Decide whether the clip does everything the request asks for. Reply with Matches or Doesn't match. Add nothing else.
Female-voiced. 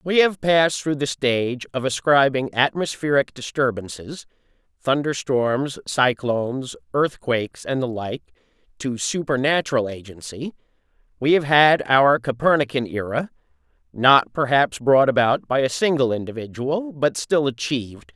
Doesn't match